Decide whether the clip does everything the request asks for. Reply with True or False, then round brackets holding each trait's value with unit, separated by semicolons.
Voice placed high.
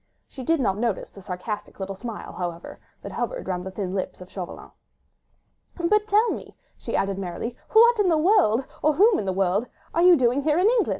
True (240 Hz)